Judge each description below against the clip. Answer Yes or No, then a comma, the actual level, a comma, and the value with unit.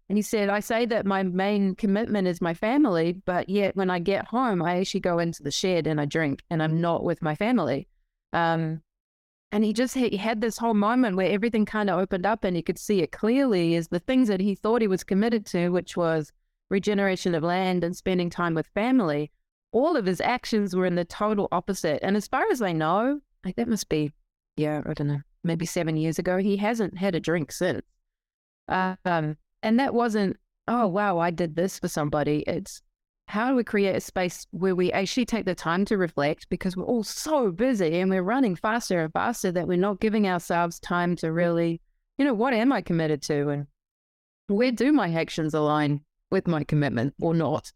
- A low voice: No, medium, 185 Hz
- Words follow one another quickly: Yes, fast, 215 wpm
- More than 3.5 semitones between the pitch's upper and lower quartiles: Yes, average, 4.2 semitones